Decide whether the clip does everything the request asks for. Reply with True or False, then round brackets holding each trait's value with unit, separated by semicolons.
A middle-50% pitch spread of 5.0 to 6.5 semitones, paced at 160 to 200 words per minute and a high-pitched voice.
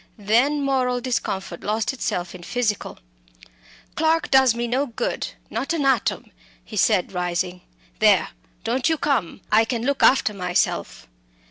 False (5.4 semitones; 140 wpm; 235 Hz)